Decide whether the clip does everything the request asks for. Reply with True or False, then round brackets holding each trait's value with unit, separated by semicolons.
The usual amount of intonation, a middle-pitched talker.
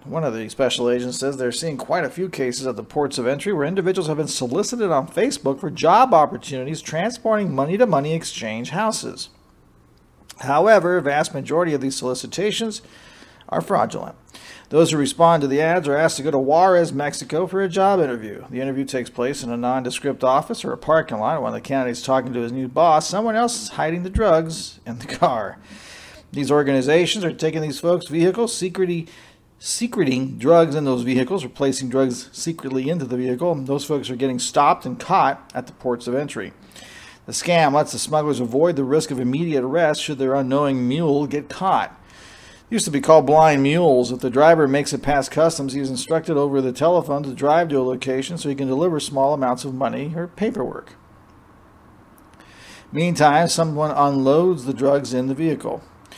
True (4.1 semitones; 145 Hz)